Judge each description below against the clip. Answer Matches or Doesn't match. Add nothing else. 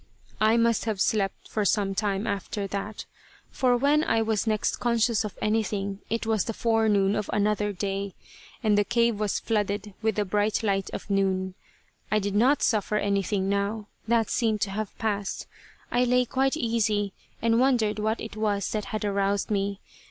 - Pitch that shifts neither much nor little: Doesn't match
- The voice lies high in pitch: Matches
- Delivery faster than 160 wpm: Matches